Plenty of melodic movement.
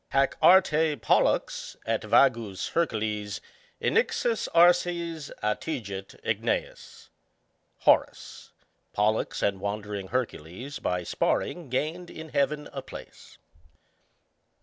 Yes: wide, 7.6 semitones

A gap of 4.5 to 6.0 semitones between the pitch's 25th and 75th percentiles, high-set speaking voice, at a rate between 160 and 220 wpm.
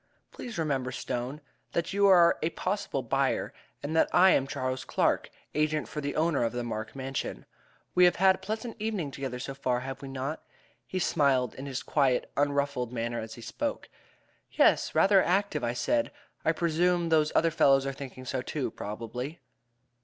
No: average, 4.8 semitones; medium, 140 Hz; average, 180 wpm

